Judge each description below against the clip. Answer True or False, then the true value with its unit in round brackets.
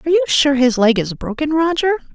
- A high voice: True (275 Hz)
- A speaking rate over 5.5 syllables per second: True (6.4 syllables/s)